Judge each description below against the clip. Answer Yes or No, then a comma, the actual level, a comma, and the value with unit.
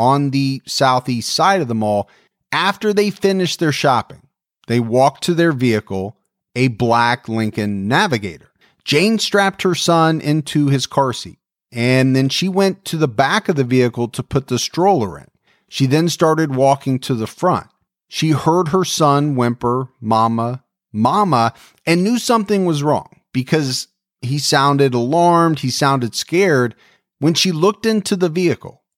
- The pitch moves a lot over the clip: Yes, wide, 6.1 semitones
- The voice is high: No, medium, 140 Hz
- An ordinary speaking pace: Yes, average, 155 wpm